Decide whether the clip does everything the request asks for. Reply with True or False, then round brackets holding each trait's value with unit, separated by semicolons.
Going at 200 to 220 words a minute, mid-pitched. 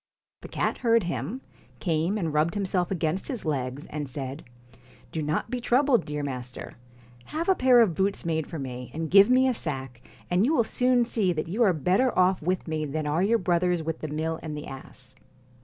True (205 wpm; 170 Hz)